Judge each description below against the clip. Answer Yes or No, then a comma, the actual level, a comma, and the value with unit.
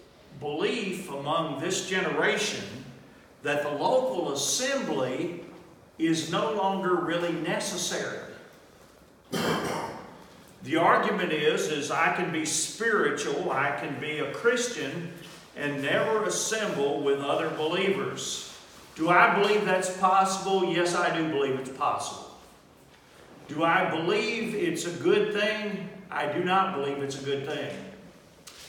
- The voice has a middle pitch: Yes, medium, 175 Hz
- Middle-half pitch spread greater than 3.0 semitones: Yes, average, 4.5 semitones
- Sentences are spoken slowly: Yes, slow, 120 wpm